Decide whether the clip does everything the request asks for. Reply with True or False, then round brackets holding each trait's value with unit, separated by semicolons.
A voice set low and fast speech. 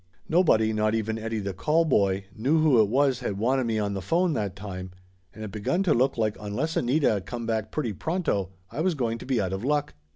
True (115 Hz; 225 wpm)